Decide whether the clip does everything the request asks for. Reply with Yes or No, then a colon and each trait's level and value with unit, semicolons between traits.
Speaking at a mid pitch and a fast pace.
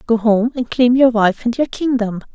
No: high, 235 Hz; fast, 230 wpm